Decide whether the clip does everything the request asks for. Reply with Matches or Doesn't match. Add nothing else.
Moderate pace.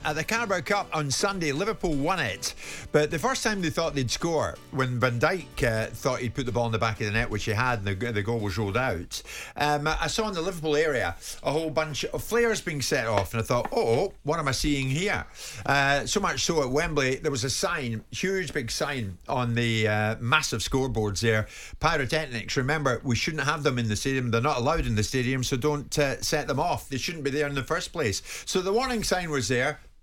Doesn't match